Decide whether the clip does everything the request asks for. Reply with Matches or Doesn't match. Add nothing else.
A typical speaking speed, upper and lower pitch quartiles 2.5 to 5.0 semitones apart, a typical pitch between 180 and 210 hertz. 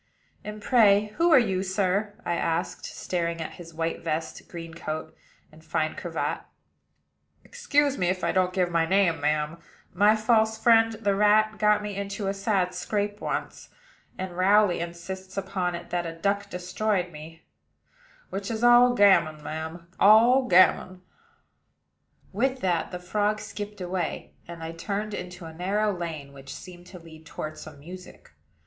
Matches